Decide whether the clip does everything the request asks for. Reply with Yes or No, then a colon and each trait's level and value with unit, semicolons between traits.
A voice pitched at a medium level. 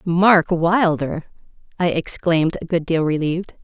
Yes: medium, 170 Hz